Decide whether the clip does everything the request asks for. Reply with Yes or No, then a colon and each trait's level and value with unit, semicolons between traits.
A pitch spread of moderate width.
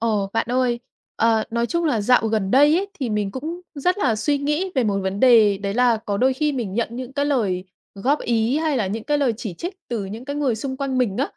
Yes: average, 4.7 semitones